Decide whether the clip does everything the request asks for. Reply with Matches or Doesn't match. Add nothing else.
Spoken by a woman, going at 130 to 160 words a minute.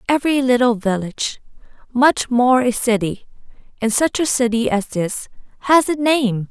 Matches